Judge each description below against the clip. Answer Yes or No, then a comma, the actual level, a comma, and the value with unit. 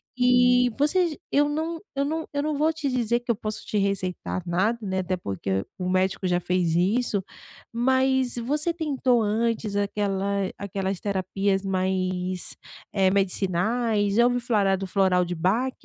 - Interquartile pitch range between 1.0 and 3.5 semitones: No, average, 4.9 semitones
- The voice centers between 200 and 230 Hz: Yes, high, 205 Hz